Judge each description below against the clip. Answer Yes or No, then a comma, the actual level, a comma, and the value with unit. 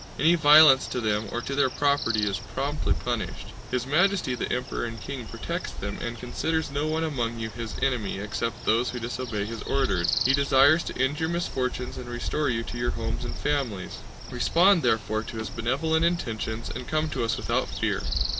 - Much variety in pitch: No, average, 4.3 semitones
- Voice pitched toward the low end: Yes, low, 125 Hz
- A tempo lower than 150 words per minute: No, average, 190 wpm